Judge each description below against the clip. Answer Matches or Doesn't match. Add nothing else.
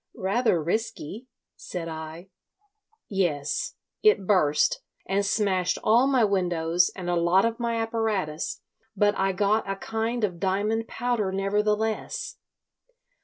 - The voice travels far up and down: Doesn't match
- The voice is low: Doesn't match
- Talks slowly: Matches